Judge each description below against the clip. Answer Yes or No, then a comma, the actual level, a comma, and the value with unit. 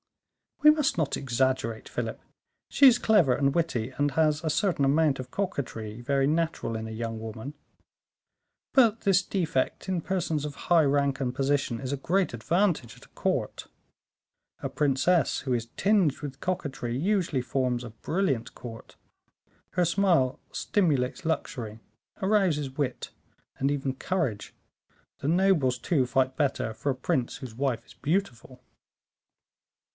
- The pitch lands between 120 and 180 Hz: Yes, medium, 140 Hz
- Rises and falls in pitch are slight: No, wide, 5.4 semitones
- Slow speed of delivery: No, average, 145 wpm